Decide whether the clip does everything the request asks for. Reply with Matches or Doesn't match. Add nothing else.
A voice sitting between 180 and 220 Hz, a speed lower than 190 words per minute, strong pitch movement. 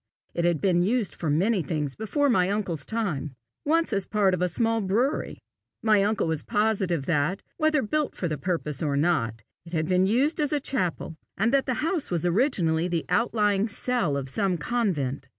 Doesn't match